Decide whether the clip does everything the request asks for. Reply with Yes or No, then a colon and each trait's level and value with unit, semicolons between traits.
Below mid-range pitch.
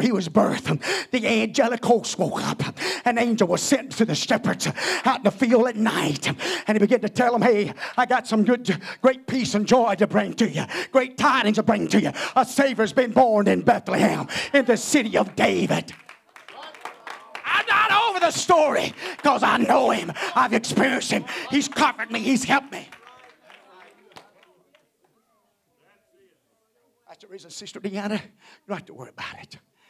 No: high, 240 Hz